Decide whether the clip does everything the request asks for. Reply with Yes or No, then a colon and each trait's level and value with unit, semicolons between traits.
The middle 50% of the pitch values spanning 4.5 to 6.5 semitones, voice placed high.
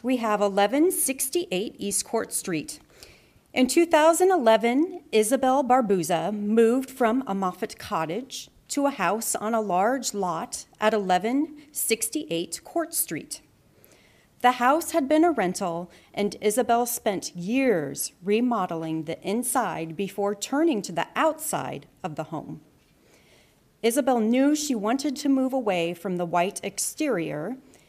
Yes: wide, 5.5 semitones; high, 230 Hz